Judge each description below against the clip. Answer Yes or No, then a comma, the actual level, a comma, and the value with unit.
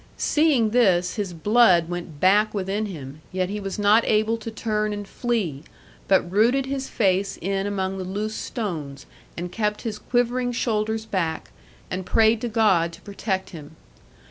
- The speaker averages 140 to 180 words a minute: Yes, average, 165 wpm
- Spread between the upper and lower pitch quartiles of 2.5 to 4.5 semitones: Yes, average, 3.4 semitones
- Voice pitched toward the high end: Yes, high, 205 Hz